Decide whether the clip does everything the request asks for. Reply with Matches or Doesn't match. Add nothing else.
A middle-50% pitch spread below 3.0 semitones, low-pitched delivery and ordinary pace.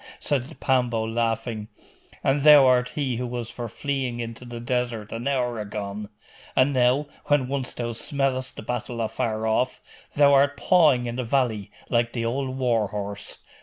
Matches